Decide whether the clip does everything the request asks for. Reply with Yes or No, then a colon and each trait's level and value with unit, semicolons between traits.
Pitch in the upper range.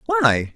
No: low, 100 Hz